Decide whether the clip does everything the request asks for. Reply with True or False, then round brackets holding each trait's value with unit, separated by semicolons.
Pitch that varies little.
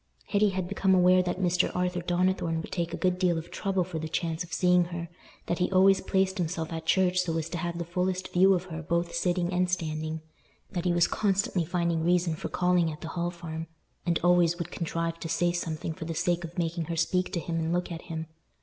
True (1.6 semitones)